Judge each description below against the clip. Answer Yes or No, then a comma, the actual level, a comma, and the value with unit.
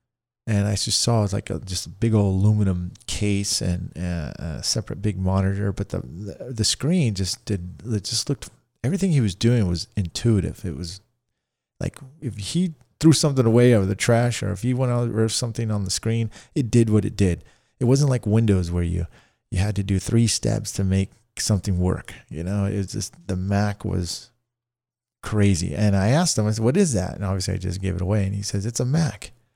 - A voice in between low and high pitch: No, low, 105 Hz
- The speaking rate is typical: No, fast, 220 wpm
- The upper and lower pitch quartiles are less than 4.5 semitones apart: Yes, average, 3.7 semitones